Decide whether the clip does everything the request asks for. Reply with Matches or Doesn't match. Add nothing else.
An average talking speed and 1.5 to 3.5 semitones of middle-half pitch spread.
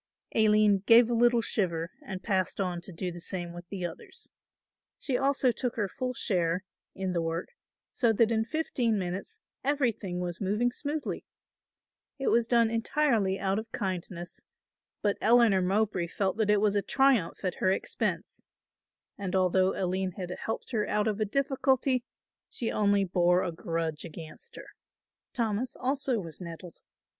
Doesn't match